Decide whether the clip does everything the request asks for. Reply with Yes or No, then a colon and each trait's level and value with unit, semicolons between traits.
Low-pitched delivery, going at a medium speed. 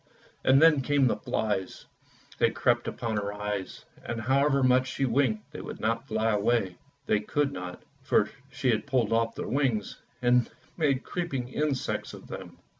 Yes: low, 120 Hz; average, 170 wpm